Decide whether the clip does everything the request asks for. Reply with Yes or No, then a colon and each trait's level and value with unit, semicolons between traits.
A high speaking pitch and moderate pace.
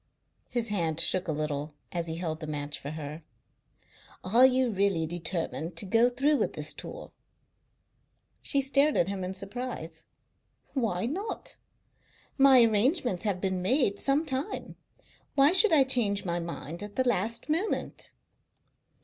Yes: high, 200 Hz; average, 150 wpm